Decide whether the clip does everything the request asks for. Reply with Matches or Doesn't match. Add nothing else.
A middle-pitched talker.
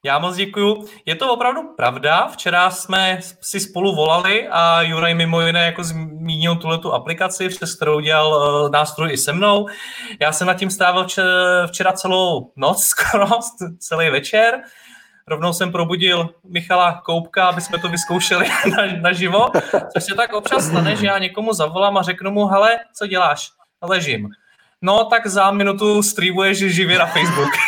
Matches